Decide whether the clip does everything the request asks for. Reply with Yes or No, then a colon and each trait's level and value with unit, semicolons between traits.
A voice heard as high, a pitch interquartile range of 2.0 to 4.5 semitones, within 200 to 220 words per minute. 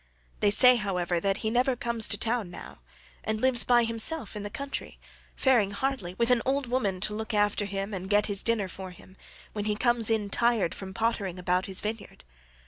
Yes: high, 215 Hz; average, 3.3 semitones; fast, 205 wpm